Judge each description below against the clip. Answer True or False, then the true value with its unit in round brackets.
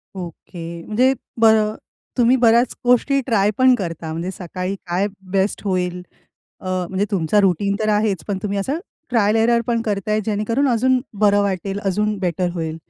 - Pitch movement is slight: False (3.7 semitones)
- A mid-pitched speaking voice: False (205 Hz)